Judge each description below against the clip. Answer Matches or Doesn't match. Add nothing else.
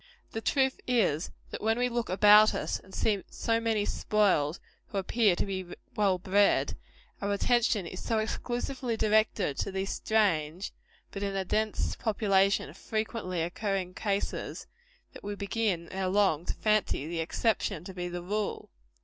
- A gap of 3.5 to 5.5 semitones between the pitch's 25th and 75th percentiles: Doesn't match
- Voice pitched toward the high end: Matches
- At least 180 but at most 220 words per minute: Doesn't match